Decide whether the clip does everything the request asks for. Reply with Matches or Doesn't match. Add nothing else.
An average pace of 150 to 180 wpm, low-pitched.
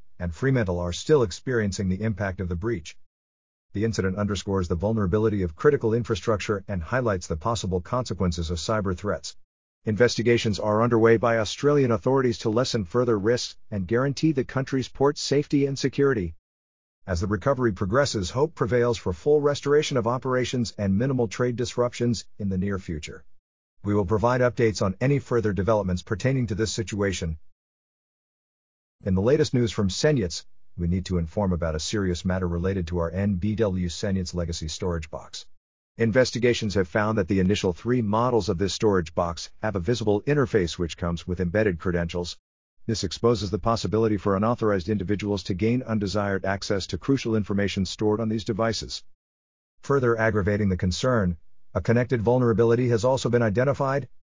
Matches